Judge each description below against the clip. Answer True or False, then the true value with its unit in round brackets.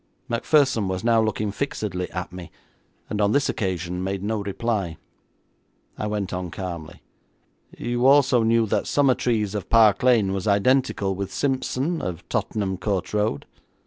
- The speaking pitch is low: True (105 Hz)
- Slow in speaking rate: False (145 wpm)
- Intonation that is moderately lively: True (4.0 semitones)